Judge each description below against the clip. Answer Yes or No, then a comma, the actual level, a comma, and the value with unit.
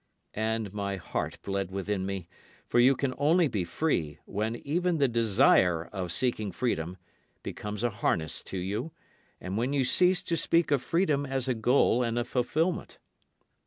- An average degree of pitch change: No, wide, 6.2 semitones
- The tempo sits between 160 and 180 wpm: Yes, average, 165 wpm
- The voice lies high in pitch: No, low, 115 Hz